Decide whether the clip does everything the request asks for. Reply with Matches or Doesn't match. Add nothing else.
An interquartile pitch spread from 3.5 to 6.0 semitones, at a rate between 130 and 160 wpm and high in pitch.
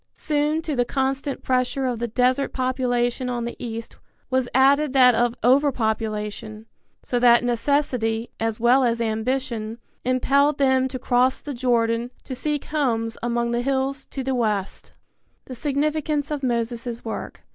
Doesn't match